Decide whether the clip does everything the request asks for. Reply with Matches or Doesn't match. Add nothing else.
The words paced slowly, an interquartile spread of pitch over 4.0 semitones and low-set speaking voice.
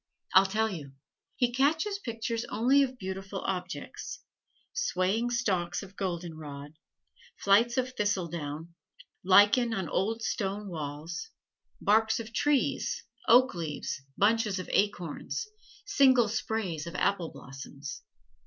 Doesn't match